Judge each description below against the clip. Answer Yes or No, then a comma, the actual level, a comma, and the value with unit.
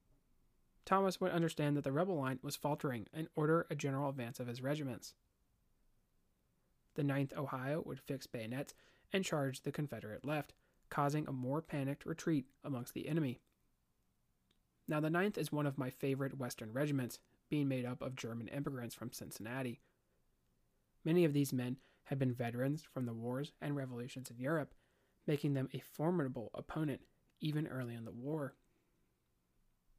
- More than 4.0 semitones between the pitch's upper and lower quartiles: No, average, 3.4 semitones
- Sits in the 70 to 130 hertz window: No, medium, 140 Hz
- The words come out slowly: No, average, 155 wpm